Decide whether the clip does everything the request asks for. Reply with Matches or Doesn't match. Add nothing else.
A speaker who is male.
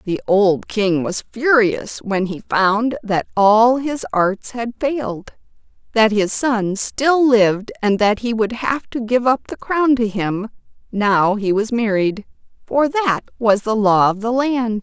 Doesn't match